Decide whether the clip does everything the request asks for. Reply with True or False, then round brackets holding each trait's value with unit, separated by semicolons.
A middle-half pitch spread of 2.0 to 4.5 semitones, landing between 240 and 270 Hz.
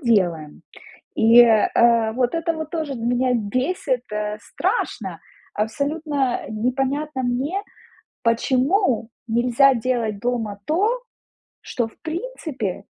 False (4.9 semitones; 250 Hz)